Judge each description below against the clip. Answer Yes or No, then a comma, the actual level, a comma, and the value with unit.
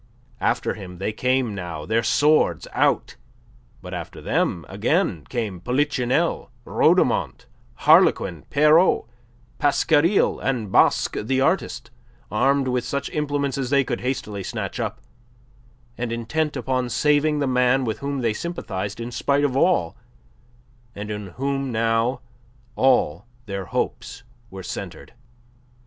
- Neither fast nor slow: No, slow, 130 wpm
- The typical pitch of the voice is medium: No, low, 125 Hz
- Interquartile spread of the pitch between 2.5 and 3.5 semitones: No, average, 4.5 semitones